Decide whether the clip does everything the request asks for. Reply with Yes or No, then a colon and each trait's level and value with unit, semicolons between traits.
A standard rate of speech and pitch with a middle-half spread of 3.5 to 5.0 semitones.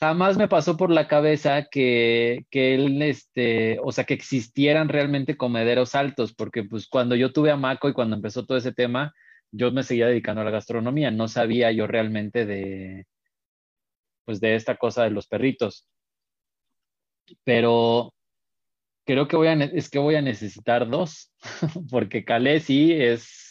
Yes: average, 165 wpm; average, 3.9 semitones